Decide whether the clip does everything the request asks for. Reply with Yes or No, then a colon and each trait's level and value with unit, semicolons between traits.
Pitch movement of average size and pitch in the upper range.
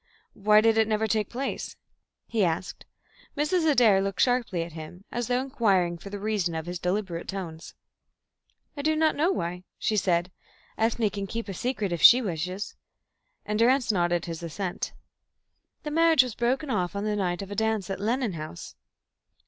Yes: average, 5.0 semitones; high, 205 Hz